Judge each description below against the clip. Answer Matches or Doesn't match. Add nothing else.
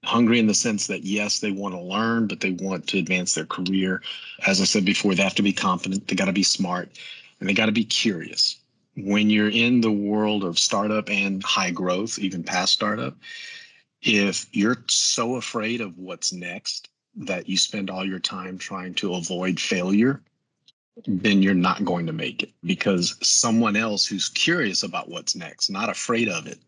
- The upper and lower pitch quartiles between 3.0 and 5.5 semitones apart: Doesn't match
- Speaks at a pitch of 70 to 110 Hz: Matches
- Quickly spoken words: Doesn't match